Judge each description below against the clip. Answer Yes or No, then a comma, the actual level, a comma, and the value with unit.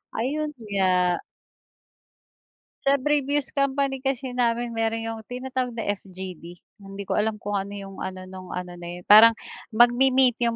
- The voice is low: No, high, 225 Hz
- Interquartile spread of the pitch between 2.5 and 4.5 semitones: No, average, 5.2 semitones